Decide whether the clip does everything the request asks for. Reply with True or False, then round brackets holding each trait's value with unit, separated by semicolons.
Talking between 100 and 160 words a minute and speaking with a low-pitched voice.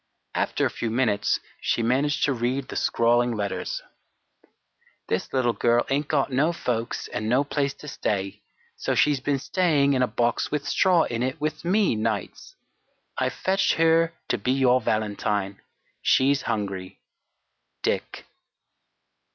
True (145 wpm; 130 Hz)